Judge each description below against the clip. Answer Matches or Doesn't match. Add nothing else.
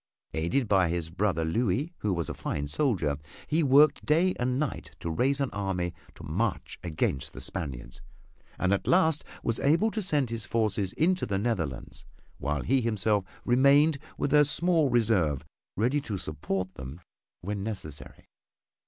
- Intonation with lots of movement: Matches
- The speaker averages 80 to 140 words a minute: Doesn't match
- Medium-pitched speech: Doesn't match